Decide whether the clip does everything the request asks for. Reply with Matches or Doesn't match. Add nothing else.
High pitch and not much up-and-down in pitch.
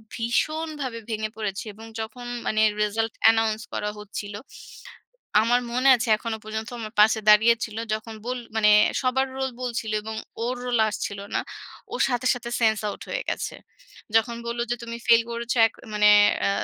Matches